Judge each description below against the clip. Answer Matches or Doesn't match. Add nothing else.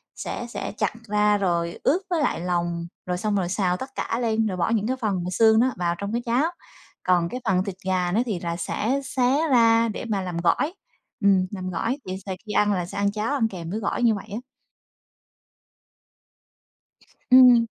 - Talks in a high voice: Matches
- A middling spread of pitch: Matches